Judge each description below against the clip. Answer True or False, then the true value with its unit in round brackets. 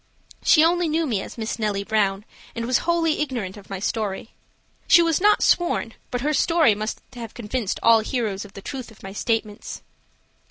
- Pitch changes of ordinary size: False (6.7 semitones)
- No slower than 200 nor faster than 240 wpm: False (190 wpm)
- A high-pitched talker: True (230 Hz)